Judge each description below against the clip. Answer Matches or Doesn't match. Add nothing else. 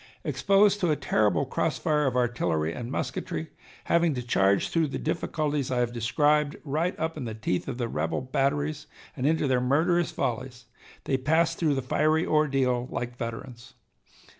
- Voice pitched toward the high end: Doesn't match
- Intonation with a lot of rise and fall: Doesn't match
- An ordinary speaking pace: Matches